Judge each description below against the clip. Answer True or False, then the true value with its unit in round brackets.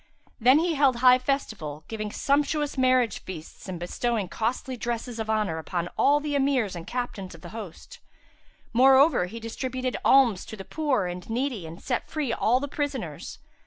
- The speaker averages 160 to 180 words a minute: True (170 wpm)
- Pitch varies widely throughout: True (5.7 semitones)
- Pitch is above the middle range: True (240 Hz)